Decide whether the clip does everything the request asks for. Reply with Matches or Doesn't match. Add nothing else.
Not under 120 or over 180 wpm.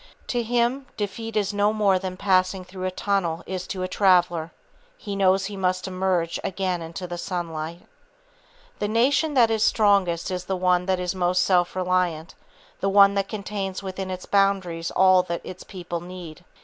Matches